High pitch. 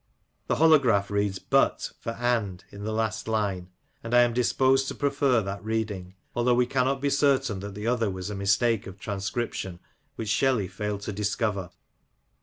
No: low, 110 Hz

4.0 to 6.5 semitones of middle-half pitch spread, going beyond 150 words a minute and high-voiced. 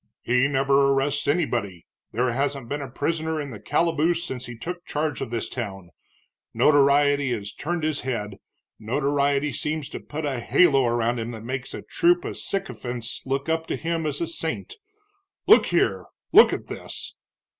No: average, 4.4 semitones; average, 170 wpm; medium, 140 Hz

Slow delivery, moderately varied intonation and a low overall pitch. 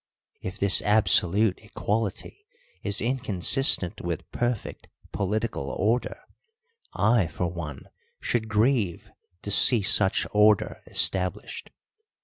Yes: slow, 100 wpm; average, 3.5 semitones; low, 105 Hz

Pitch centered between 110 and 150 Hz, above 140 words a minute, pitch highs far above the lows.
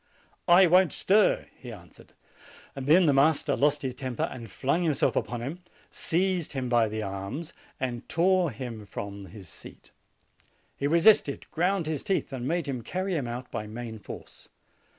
Yes: low, 135 Hz; average, 165 wpm; wide, 6.3 semitones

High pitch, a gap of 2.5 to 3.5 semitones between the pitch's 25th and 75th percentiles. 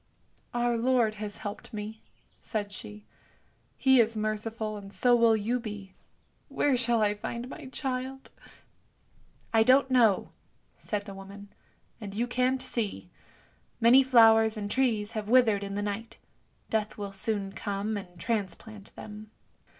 Yes: high, 220 Hz; average, 2.8 semitones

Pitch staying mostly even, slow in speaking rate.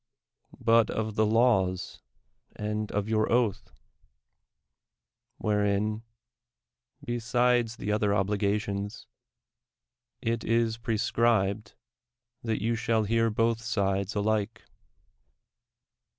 Yes: narrow, 1.9 semitones; slow, 90 wpm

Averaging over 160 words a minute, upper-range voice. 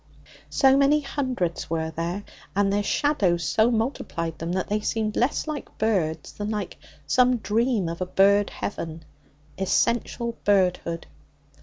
No: average, 140 wpm; high, 205 Hz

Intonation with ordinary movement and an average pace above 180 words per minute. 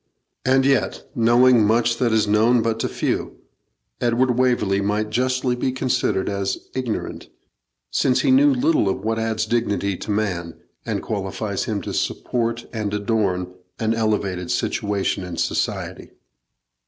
No: average, 3.3 semitones; average, 140 wpm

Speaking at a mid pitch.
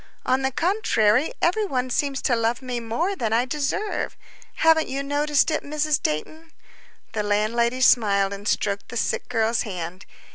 No: very high, 250 Hz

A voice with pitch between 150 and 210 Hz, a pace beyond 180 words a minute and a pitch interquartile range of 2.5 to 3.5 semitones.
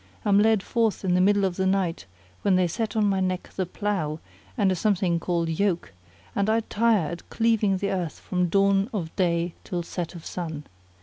Yes: high, 190 Hz; average, 200 wpm; average, 2.9 semitones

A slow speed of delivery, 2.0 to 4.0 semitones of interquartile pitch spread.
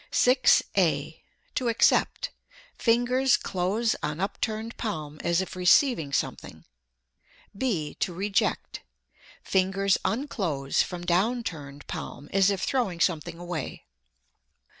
No: slow, 110 wpm; wide, 5.6 semitones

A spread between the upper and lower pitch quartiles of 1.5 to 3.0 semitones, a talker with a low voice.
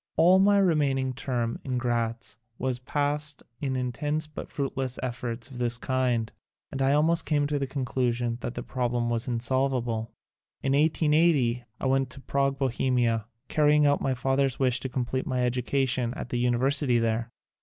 Yes: narrow, 2.6 semitones; low, 130 Hz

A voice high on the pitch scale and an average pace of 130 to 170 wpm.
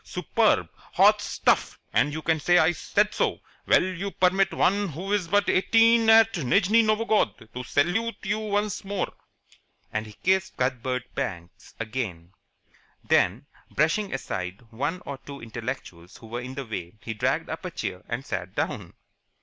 No: medium, 160 Hz; average, 160 wpm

